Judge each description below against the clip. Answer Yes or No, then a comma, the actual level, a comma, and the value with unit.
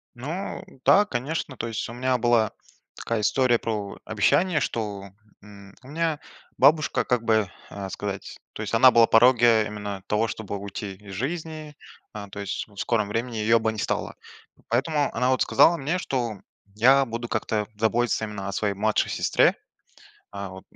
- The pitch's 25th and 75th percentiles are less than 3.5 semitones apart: No, average, 3.8 semitones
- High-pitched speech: No, low, 115 Hz